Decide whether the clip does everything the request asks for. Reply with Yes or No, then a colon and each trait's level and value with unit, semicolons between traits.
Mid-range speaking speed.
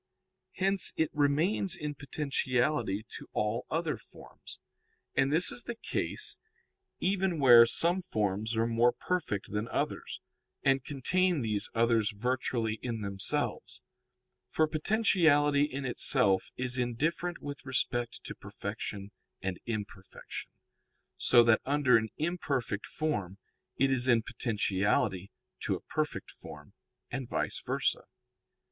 No: slow, 125 wpm